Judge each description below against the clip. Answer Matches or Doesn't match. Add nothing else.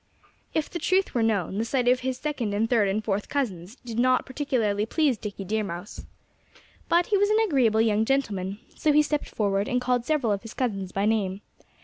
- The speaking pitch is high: Matches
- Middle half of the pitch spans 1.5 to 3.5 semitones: Doesn't match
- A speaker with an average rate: Doesn't match